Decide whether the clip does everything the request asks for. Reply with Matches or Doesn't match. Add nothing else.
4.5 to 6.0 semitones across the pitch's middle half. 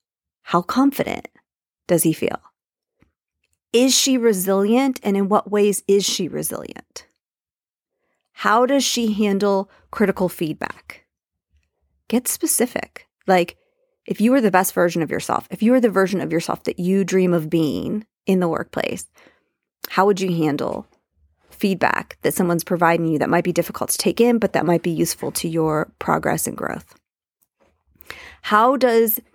Matches